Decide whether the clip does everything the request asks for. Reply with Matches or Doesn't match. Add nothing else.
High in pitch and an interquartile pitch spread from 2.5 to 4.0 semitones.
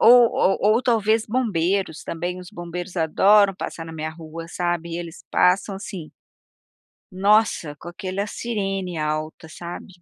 Doesn't match